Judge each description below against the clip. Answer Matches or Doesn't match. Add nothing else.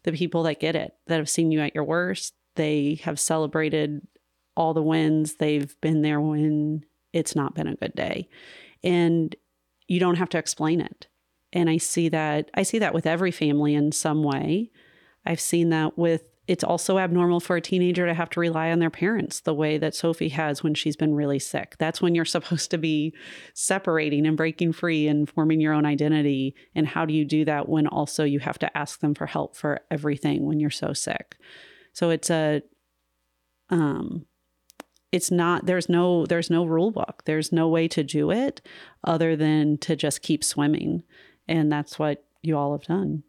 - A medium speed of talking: Matches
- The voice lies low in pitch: Doesn't match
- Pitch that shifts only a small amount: Matches